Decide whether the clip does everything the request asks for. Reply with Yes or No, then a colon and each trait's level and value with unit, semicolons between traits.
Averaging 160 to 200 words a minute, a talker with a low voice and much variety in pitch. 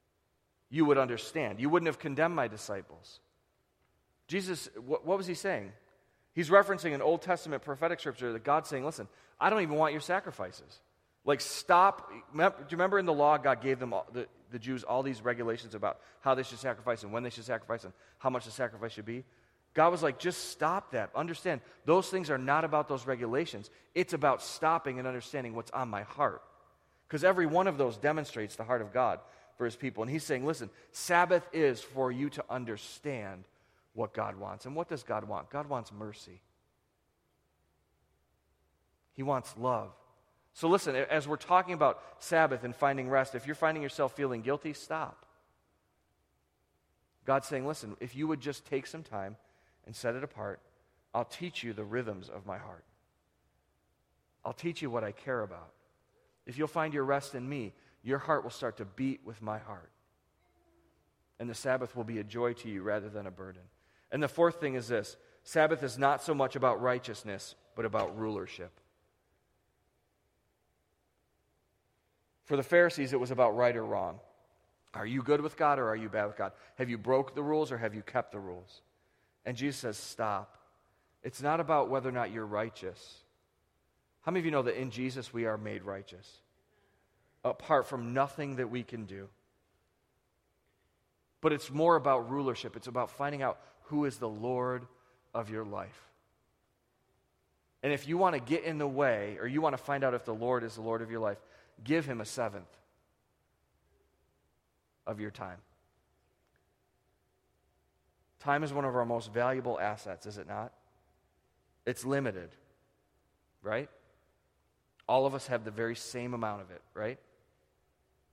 Yes: average, 180 wpm; low, 125 Hz; wide, 5.7 semitones